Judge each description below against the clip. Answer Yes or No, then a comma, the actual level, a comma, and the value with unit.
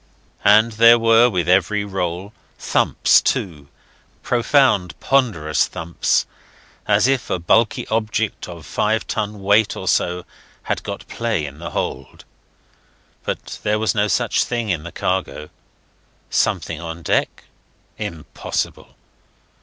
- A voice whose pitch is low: Yes, low, 100 Hz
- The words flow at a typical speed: No, slow, 125 wpm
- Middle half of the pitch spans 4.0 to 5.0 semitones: Yes, average, 4.6 semitones